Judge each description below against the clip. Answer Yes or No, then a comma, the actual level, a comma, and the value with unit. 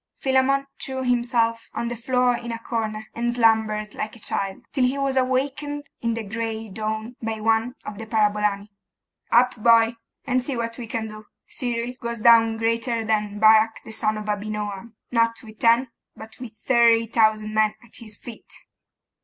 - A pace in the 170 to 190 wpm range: Yes, average, 175 wpm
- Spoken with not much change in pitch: Yes, narrow, 1.8 semitones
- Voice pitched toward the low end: No, high, 230 Hz